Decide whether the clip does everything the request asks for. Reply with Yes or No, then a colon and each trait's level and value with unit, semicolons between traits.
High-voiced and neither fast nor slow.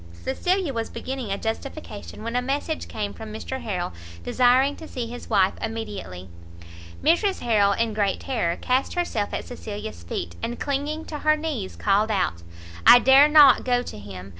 Yes: high, 235 Hz; average, 170 wpm